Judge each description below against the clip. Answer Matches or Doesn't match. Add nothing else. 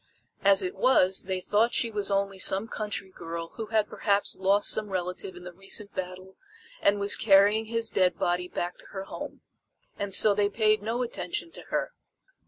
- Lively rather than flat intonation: Doesn't match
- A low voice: Doesn't match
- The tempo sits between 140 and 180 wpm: Doesn't match